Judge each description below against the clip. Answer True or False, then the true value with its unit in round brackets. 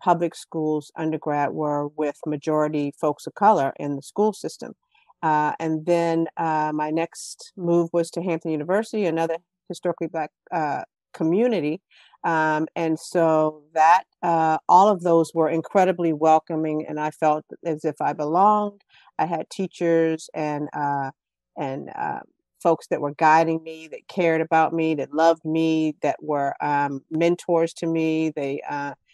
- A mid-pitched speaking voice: True (160 Hz)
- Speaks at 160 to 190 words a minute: False (150 wpm)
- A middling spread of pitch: False (1.7 semitones)